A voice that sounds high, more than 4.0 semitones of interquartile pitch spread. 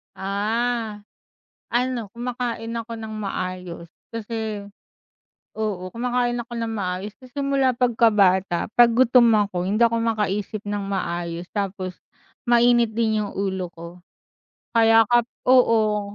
No: high, 220 Hz; average, 3.4 semitones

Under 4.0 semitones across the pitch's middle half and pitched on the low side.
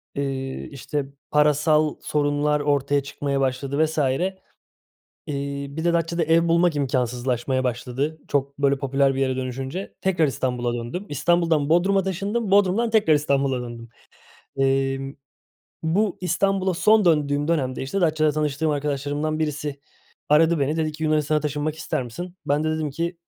No: average, 3.4 semitones; medium, 150 Hz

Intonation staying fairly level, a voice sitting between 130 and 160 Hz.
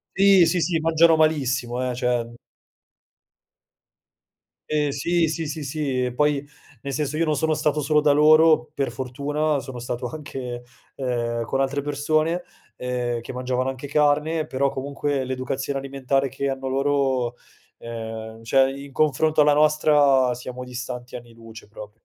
No: average, 3.2 semitones; low, 135 Hz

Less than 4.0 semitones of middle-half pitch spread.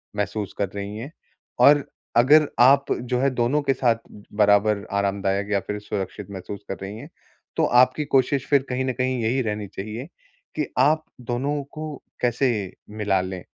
No: average, 4.6 semitones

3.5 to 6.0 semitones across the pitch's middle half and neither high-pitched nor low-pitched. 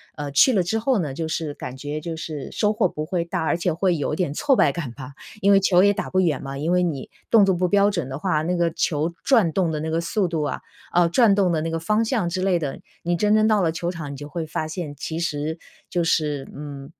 Yes: average, 3.9 semitones; medium, 170 Hz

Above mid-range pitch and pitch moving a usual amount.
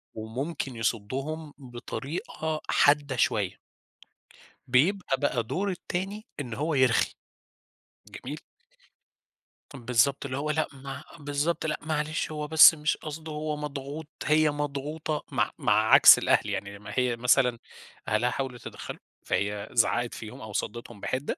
No: medium, 140 Hz; average, 4.0 semitones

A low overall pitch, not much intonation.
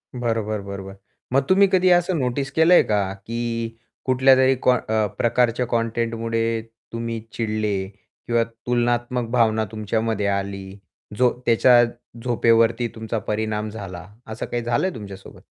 Yes: low, 115 Hz; narrow, 2.1 semitones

